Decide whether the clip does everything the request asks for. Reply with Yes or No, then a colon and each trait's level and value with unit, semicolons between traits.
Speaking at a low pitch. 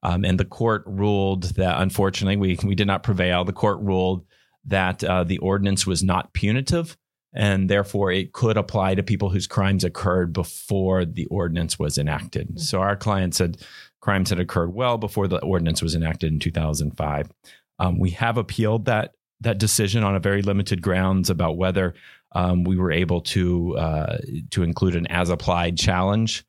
Yes: very low, 95 Hz